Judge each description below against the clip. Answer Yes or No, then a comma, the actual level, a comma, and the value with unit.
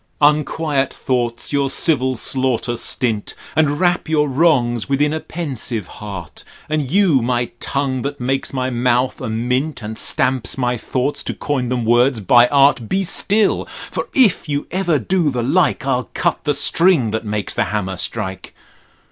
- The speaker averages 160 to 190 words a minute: Yes, average, 165 wpm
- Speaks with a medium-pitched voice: No, low, 130 Hz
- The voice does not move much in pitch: No, average, 3.8 semitones